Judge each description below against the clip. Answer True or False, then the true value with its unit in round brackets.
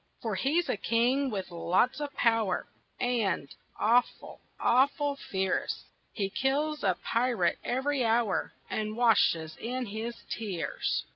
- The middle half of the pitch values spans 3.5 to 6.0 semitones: True (4.8 semitones)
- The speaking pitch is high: True (230 Hz)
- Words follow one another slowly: True (125 wpm)